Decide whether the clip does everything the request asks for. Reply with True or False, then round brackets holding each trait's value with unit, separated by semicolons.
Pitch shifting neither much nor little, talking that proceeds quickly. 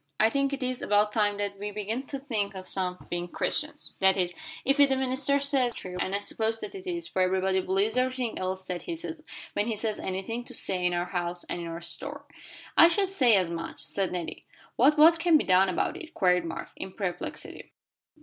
False (6.6 semitones; 225 wpm)